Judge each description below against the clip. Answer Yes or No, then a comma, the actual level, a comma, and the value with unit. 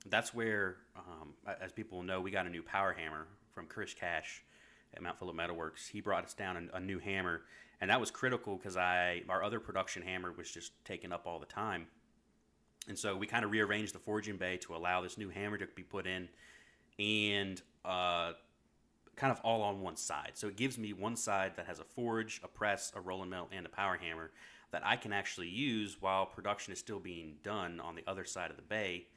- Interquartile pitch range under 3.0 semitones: Yes, narrow, 2.5 semitones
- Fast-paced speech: Yes, fast, 220 wpm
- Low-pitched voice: Yes, very low, 95 Hz